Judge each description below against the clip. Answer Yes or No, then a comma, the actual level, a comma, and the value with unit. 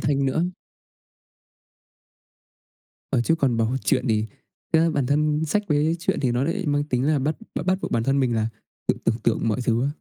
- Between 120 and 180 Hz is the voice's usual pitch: Yes, medium, 140 Hz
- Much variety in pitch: No, average, 4.4 semitones